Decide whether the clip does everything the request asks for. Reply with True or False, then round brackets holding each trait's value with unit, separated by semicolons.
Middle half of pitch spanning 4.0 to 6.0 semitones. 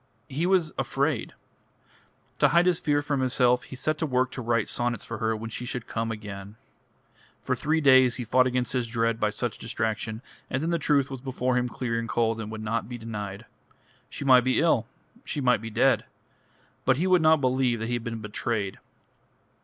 False (3.0 semitones)